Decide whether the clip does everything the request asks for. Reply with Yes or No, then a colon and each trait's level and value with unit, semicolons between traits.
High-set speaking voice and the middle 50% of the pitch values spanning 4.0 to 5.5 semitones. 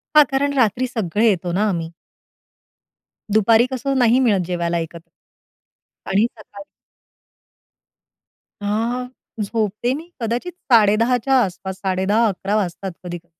Yes: high, 210 Hz; average, 4.3 semitones